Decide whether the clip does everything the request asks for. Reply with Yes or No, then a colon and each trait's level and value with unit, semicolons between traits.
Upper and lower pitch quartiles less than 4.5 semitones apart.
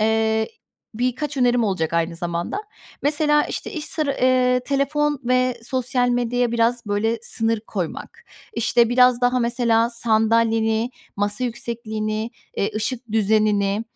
Yes: narrow, 2.5 semitones